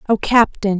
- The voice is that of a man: No, female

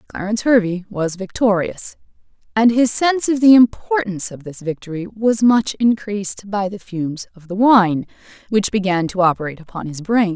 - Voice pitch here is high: Yes, high, 200 Hz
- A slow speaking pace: No, average, 170 wpm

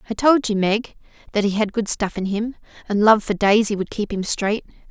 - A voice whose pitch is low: No, high, 210 Hz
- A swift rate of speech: Yes, fast, 235 wpm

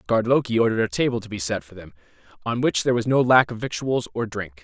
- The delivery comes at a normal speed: No, fast, 260 wpm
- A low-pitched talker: Yes, low, 115 Hz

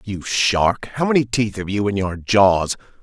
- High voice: No, low, 105 Hz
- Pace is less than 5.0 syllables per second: Yes, 4.2 syllables/s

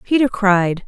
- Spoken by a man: No, female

